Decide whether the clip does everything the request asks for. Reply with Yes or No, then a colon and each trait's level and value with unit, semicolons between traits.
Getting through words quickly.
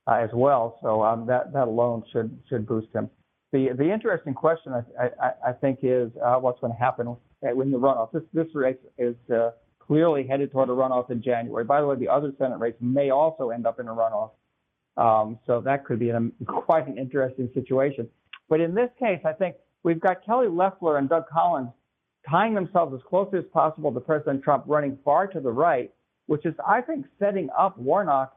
Yes: fast, 210 wpm